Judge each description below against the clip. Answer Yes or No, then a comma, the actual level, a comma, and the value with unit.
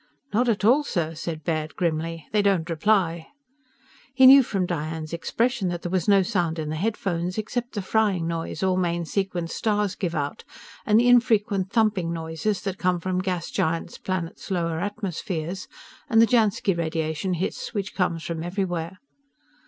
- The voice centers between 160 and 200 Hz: Yes, medium, 185 Hz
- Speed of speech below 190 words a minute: Yes, average, 170 wpm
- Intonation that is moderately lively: Yes, average, 3.9 semitones